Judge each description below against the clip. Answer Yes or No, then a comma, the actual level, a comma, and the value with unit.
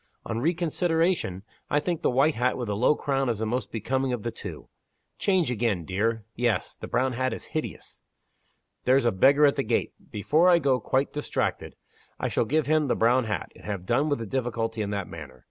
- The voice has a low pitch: Yes, low, 125 Hz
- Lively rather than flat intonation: No, average, 4.9 semitones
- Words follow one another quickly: Yes, fast, 210 wpm